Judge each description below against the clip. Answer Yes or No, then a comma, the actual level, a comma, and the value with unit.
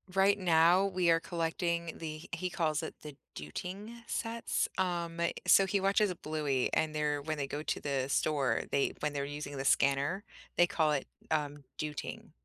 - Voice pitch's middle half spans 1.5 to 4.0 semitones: Yes, average, 3.6 semitones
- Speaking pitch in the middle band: Yes, medium, 160 Hz